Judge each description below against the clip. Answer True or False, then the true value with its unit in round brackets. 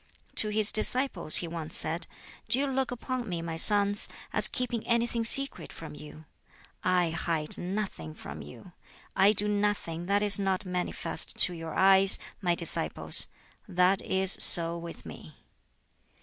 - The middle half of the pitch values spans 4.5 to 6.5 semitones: False (4.0 semitones)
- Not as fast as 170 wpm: True (150 wpm)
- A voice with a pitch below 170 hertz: False (190 Hz)